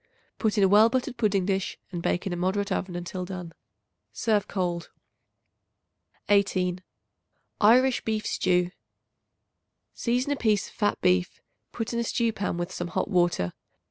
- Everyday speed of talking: Yes, average, 155 wpm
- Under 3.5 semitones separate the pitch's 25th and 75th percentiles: No, average, 3.8 semitones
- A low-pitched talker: No, high, 195 Hz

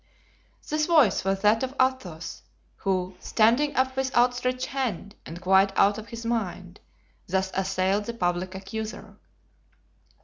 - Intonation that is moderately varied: Yes, average, 5.0 semitones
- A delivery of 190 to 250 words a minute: No, slow, 135 wpm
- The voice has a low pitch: No, high, 210 Hz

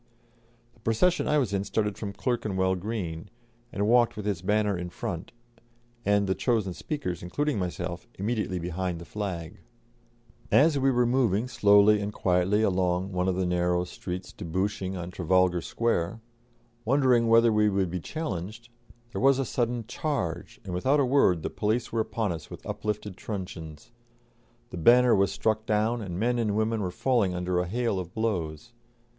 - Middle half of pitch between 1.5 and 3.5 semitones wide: No, average, 4.4 semitones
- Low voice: Yes, low, 100 Hz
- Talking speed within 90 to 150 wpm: No, average, 170 wpm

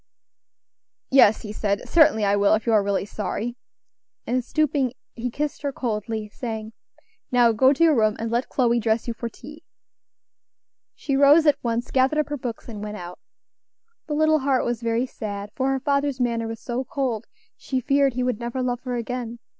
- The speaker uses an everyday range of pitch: Yes, average, 3.4 semitones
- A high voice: Yes, high, 240 Hz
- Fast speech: No, average, 190 wpm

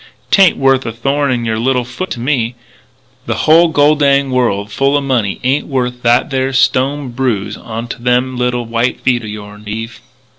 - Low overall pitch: Yes, low, 125 Hz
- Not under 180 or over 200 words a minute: Yes, average, 185 wpm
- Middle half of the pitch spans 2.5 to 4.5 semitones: Yes, average, 2.8 semitones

